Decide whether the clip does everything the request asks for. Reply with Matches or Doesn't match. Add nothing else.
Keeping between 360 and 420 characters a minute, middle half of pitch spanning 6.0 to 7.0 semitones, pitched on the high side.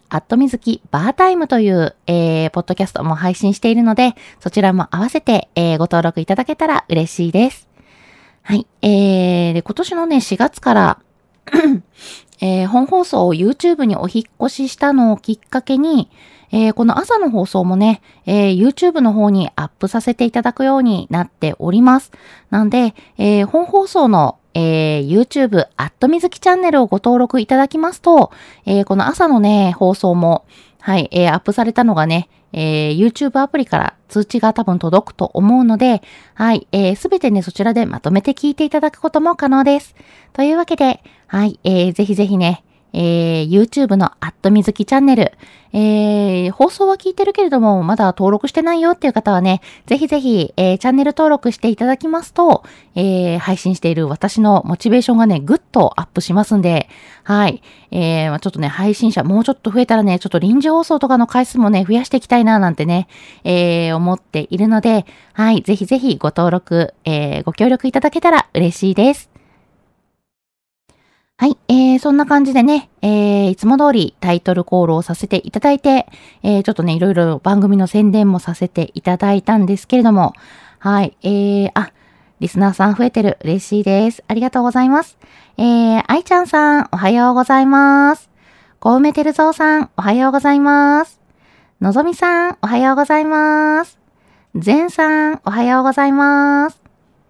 Matches